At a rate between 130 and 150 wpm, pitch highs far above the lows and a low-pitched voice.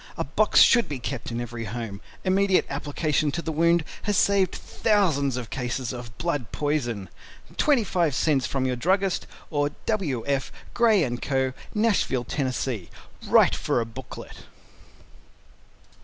No: average, 140 wpm; wide, 7.0 semitones; medium, 145 Hz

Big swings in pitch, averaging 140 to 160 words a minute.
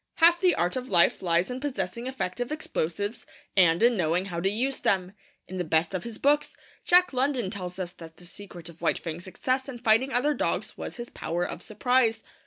No: wide, 6.5 semitones; fast, 205 wpm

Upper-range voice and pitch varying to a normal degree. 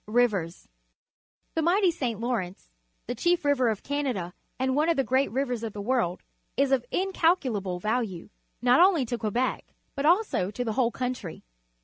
Yes: very high, 250 Hz; average, 4.9 semitones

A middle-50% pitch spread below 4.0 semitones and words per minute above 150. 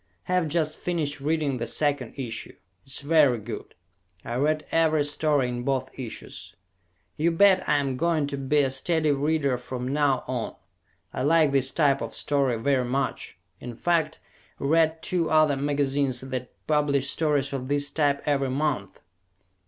Yes: average, 2.8 semitones; average, 160 wpm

